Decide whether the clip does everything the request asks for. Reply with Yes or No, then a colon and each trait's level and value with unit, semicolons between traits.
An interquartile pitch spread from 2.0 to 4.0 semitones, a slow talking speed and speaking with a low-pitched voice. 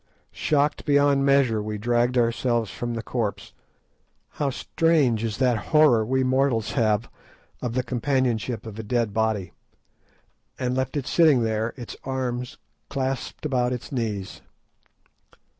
Yes: average, 3.0 semitones; slow, 125 wpm; low, 125 Hz